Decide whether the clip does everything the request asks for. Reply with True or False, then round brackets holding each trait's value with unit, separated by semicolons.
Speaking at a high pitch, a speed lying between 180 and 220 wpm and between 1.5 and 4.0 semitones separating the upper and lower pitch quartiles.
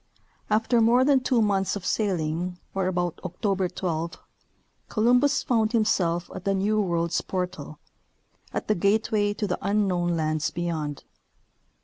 False (195 Hz; 140 wpm; 3.7 semitones)